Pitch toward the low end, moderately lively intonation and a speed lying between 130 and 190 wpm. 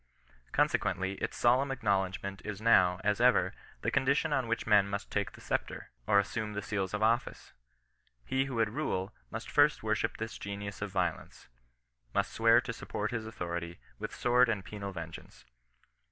Yes: low, 105 Hz; average, 3.5 semitones; average, 180 wpm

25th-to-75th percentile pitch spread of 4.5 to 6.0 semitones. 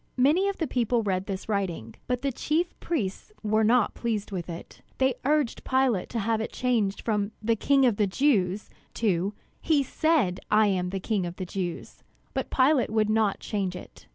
Yes: average, 5.0 semitones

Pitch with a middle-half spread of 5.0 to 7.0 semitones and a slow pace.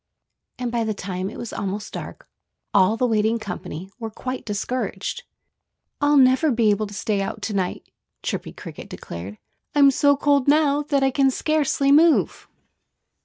No: wide, 5.4 semitones; average, 165 wpm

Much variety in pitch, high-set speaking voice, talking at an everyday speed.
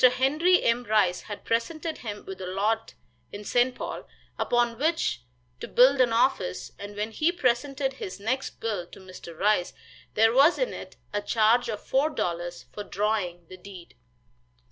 No: average, 4.7 semitones; high, 225 Hz; average, 165 wpm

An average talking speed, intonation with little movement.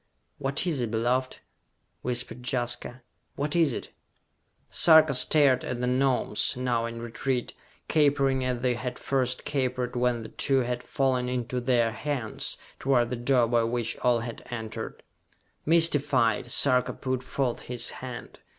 Yes: average, 145 wpm; narrow, 1.9 semitones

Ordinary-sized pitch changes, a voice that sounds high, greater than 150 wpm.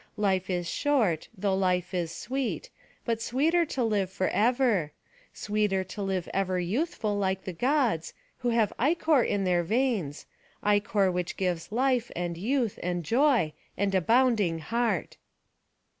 No: average, 5.0 semitones; high, 205 Hz; average, 145 wpm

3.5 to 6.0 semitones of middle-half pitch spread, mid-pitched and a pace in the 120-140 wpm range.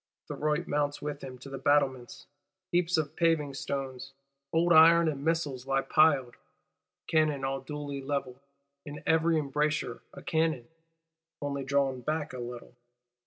No: average, 3.0 semitones; medium, 145 Hz; slow, 135 wpm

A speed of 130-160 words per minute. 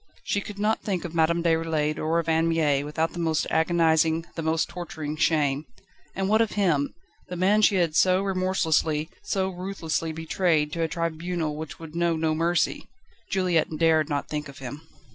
No: average, 180 wpm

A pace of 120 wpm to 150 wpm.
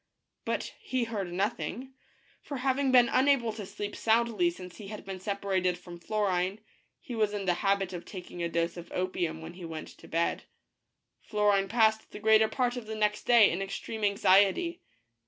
No: average, 195 wpm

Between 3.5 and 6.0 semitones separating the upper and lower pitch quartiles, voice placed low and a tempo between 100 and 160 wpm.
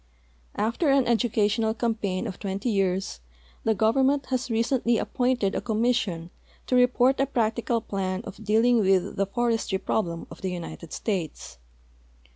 No: average, 3.9 semitones; high, 220 Hz; average, 145 wpm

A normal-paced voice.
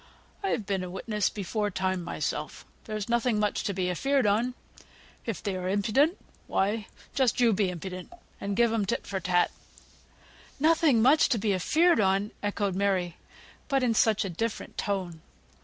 Yes: average, 165 wpm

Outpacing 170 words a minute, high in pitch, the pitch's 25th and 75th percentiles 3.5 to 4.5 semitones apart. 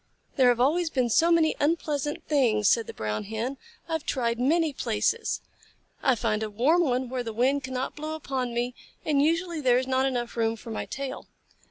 Yes: average, 200 wpm; very high, 260 Hz; average, 4.2 semitones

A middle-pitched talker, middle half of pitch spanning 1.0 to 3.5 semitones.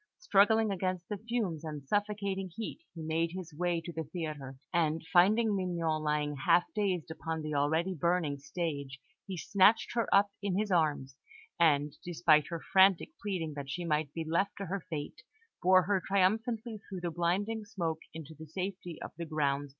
No: medium, 170 Hz; average, 4.0 semitones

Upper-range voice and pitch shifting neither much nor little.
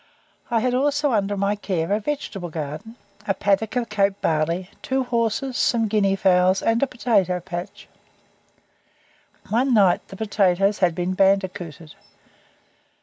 Yes: high, 200 Hz; average, 4.0 semitones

